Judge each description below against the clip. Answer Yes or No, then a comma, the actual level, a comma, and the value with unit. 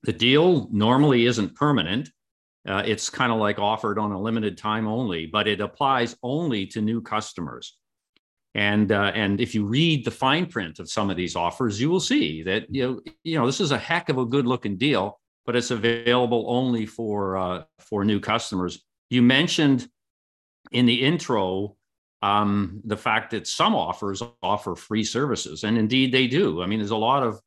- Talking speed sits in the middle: Yes, average, 190 wpm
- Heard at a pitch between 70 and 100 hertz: No, low, 110 Hz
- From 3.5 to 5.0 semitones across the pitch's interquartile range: Yes, average, 3.8 semitones